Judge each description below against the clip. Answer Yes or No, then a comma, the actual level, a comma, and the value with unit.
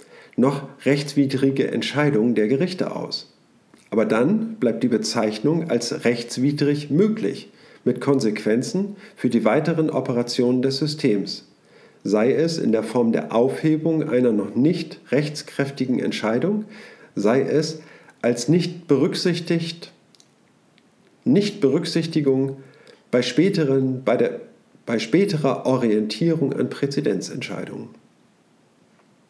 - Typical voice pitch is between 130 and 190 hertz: Yes, medium, 140 Hz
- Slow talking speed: Yes, slow, 95 wpm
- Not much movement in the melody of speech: No, average, 4.7 semitones